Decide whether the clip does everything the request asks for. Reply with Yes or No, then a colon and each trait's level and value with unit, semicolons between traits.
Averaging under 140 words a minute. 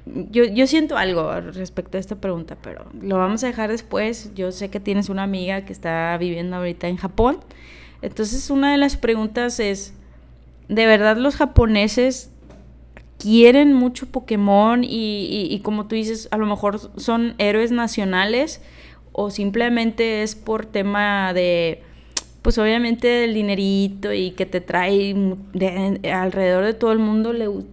No: average, 170 wpm